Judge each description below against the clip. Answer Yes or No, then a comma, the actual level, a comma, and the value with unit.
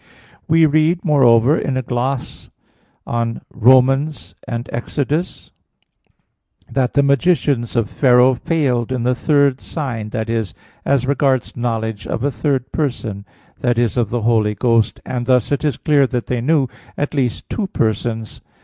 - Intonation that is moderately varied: Yes, average, 3.3 semitones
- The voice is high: No, low, 125 Hz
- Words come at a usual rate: Yes, average, 155 wpm